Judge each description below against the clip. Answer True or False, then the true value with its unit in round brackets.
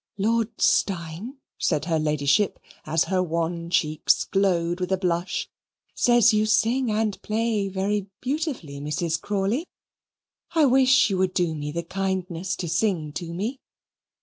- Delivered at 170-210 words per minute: False (145 wpm)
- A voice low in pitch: False (190 Hz)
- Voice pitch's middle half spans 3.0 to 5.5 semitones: True (4.5 semitones)